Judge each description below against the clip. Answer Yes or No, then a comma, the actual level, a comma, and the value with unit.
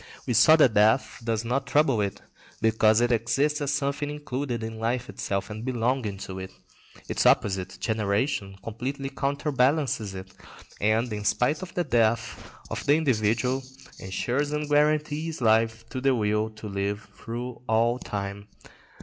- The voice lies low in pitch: Yes, low, 120 Hz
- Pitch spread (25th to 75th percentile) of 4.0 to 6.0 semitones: Yes, average, 4.4 semitones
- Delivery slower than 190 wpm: Yes, average, 150 wpm